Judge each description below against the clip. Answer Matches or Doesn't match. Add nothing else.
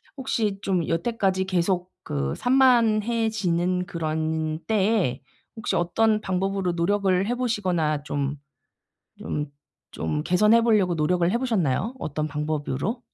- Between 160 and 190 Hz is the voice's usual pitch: Matches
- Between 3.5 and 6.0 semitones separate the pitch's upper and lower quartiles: Matches